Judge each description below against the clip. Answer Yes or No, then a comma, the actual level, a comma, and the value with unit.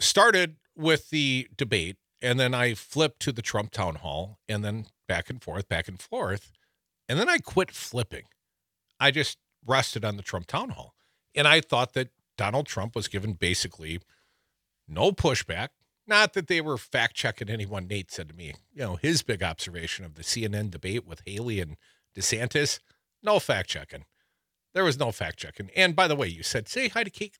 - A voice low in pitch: Yes, low, 110 Hz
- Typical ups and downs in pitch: No, wide, 6.8 semitones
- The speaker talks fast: No, average, 190 wpm